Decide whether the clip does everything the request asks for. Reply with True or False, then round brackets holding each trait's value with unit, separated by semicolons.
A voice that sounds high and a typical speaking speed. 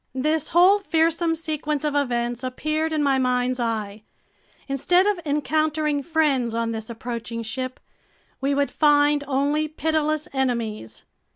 False (285 Hz; 130 wpm)